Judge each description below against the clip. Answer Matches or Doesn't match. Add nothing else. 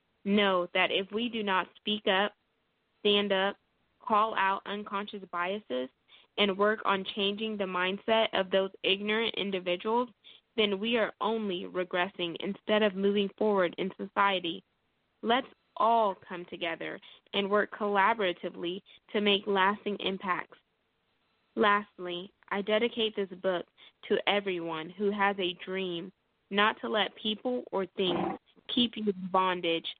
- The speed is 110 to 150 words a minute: Matches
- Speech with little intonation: Matches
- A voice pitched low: Doesn't match